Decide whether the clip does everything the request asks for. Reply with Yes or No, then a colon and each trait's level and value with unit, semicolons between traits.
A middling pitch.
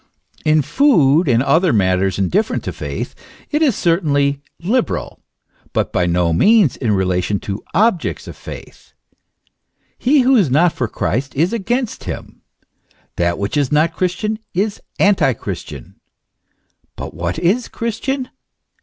Yes: medium, 160 Hz